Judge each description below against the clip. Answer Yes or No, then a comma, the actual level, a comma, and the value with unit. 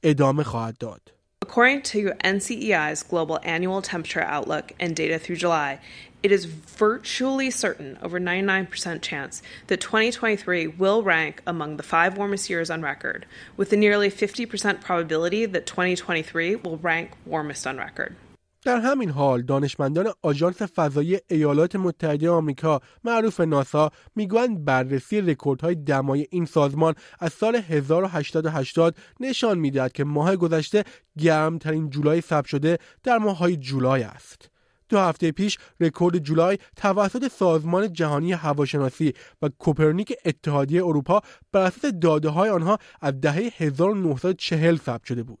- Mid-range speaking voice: Yes, medium, 170 Hz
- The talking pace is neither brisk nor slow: Yes, average, 130 wpm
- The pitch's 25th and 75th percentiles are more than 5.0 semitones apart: No, average, 4.7 semitones